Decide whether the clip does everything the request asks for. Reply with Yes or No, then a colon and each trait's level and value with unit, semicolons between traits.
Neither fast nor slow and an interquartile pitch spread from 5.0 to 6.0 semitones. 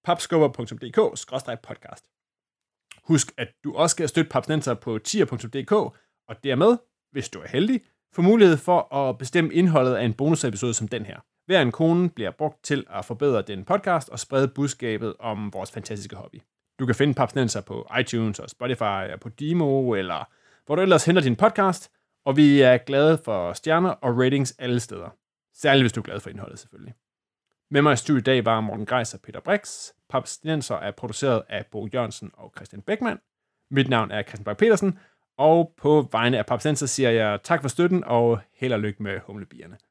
Yes: average, 185 wpm; wide, 5.6 semitones